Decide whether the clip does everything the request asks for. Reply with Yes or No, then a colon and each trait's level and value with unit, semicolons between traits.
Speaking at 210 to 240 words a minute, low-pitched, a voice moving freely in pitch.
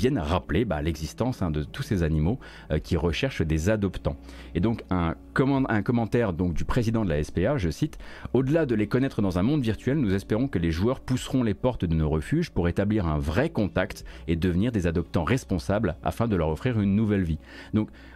Yes: average, 215 wpm; very low, 95 Hz; wide, 6.1 semitones